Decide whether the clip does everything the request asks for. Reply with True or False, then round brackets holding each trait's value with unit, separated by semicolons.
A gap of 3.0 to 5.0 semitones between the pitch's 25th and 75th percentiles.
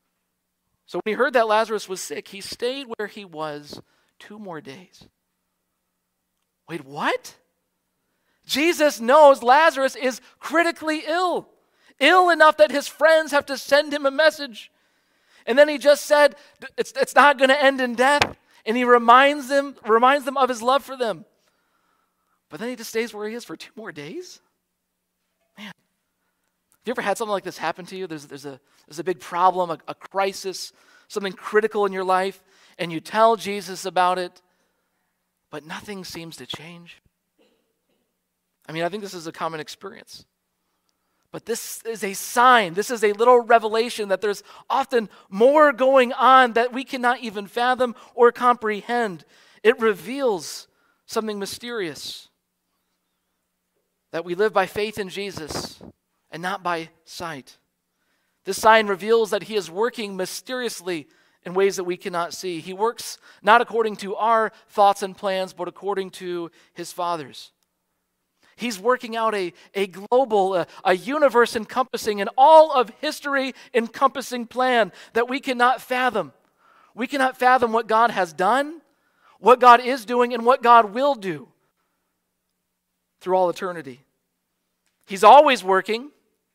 False (5.6 semitones)